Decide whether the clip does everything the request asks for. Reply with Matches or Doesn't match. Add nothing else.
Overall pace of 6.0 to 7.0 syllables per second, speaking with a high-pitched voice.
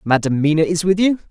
Doesn't match